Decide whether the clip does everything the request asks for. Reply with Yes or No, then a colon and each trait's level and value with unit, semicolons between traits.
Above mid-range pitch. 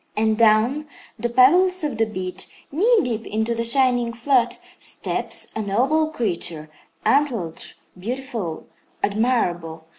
Yes: high, 230 Hz